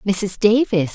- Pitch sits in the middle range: No, high, 200 Hz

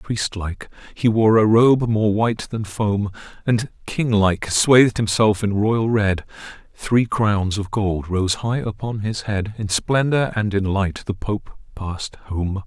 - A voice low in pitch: Yes, low, 105 Hz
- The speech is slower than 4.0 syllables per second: Yes, 3.8 syllables/s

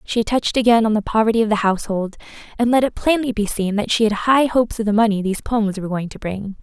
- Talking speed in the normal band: No, fast, 265 wpm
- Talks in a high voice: Yes, high, 220 Hz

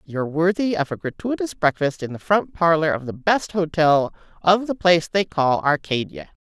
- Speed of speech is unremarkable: Yes, average, 185 wpm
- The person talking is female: Yes, female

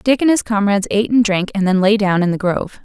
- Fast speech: Yes, fast, 295 wpm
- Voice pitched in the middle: No, high, 205 Hz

